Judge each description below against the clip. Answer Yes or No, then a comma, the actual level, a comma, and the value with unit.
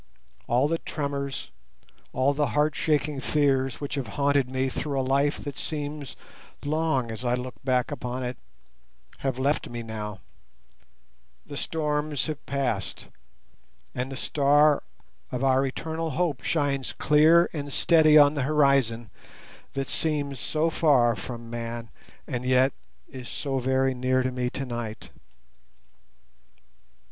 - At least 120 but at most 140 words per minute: Yes, slow, 135 wpm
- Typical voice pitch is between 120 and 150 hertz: Yes, low, 135 Hz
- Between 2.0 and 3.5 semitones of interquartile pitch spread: Yes, average, 2.7 semitones